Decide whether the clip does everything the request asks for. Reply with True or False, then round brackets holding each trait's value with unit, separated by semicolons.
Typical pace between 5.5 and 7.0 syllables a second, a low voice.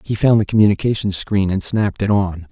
True (5.8 syllables/s; 100 Hz)